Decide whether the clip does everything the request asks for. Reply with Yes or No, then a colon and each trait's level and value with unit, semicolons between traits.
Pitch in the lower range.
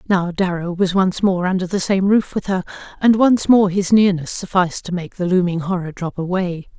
No: medium, 185 Hz